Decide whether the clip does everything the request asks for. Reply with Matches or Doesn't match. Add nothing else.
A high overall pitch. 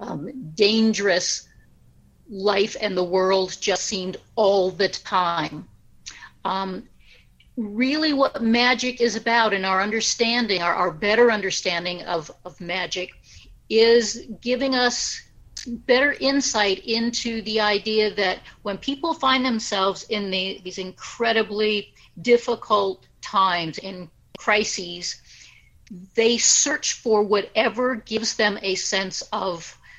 Matches